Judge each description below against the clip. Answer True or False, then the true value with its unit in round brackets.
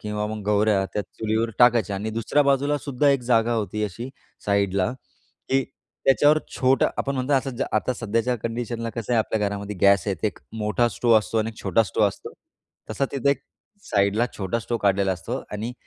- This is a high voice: False (110 Hz)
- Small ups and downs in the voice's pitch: False (3.0 semitones)